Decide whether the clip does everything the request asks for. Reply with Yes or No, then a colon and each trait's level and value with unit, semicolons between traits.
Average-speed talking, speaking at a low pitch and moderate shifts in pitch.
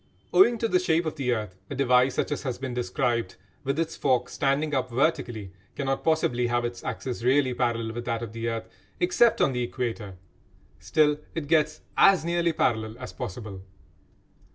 Yes: average, 180 wpm; low, 130 Hz; average, 4.3 semitones